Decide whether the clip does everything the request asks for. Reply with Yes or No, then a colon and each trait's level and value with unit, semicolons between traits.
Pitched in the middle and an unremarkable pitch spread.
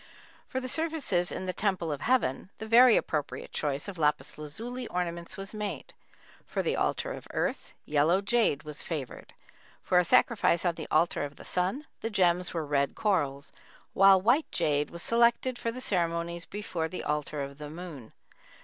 No: medium, 175 Hz; wide, 6.1 semitones